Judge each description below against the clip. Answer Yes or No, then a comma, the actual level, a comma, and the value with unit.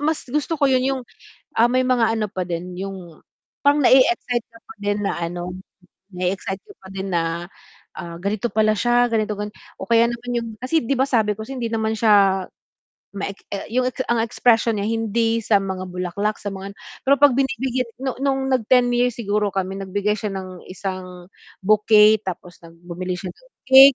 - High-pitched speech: Yes, high, 215 Hz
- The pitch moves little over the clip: No, average, 4.3 semitones